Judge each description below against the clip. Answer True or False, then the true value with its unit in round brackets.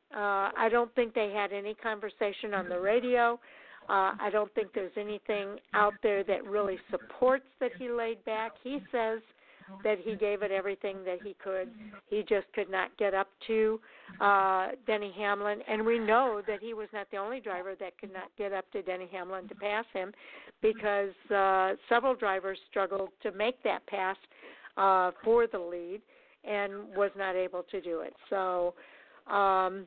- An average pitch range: False (2.3 semitones)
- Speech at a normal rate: True (180 wpm)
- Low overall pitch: False (205 Hz)